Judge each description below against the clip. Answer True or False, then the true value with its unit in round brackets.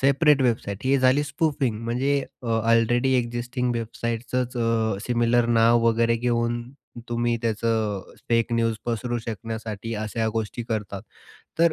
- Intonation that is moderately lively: False (1.5 semitones)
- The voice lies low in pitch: True (115 Hz)